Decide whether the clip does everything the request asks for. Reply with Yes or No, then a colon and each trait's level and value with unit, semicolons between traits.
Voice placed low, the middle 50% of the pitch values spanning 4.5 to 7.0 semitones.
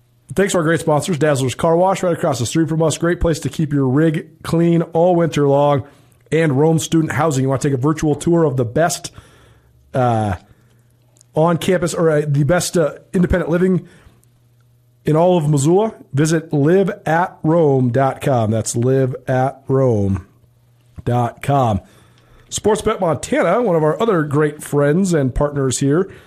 No: medium, 150 Hz; average, 4.9 semitones